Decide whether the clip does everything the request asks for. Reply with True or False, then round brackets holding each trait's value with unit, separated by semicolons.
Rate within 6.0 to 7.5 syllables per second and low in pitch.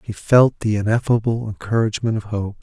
False (5.8 syllables/s; 110 Hz)